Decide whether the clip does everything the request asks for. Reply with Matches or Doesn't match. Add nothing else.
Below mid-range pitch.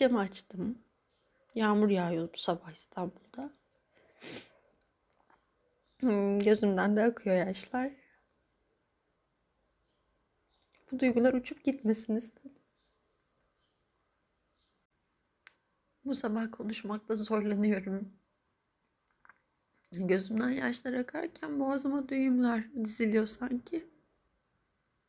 Doesn't match